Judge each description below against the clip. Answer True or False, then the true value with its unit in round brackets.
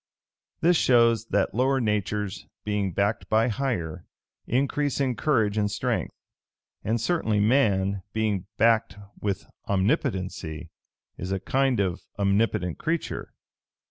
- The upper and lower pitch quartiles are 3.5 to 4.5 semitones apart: True (4.2 semitones)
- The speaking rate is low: True (115 wpm)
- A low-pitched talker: True (105 Hz)